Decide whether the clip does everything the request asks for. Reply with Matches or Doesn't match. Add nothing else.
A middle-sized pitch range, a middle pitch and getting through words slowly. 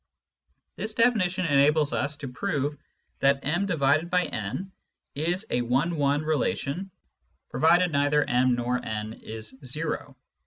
Matches